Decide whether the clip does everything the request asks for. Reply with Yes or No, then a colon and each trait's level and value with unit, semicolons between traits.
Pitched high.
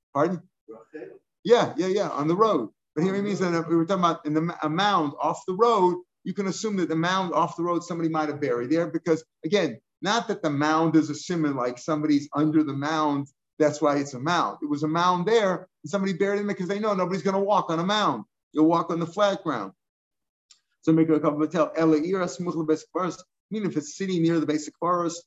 No: medium, 165 Hz